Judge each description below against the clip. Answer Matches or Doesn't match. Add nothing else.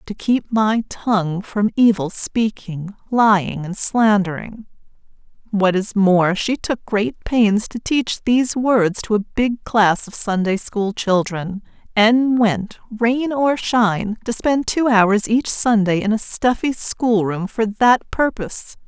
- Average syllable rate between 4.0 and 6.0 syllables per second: Doesn't match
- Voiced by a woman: Matches